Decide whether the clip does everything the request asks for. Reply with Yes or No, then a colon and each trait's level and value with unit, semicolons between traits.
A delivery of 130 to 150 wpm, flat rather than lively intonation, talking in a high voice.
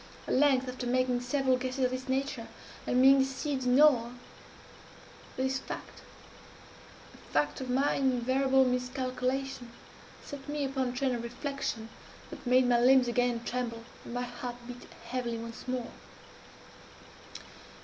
Yes: average, 140 wpm; narrow, 1.4 semitones; very high, 255 Hz